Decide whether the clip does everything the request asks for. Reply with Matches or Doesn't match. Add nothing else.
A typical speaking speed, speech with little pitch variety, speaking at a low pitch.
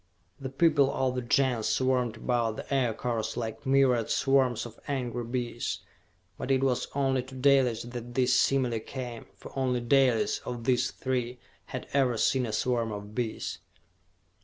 Matches